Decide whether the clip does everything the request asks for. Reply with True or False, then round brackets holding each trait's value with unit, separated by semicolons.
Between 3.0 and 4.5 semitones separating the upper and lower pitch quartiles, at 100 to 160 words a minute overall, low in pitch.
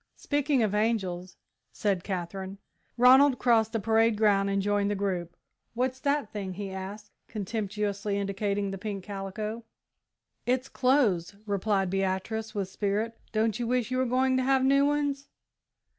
False (4.0 semitones; 155 wpm; 210 Hz)